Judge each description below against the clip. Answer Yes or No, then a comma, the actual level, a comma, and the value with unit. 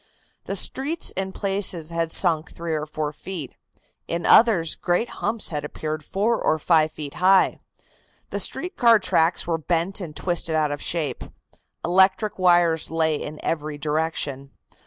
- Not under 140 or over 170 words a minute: Yes, average, 155 wpm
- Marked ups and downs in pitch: No, average, 3.5 semitones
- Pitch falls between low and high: Yes, medium, 165 Hz